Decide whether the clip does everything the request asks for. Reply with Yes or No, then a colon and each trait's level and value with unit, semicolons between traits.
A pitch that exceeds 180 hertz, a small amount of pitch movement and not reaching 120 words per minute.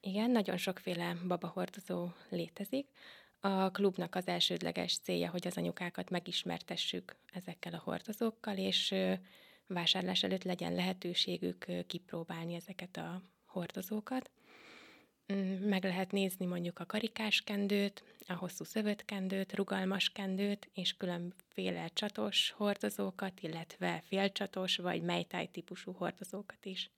Yes: high, 190 Hz; narrow, 2.3 semitones; average, 110 wpm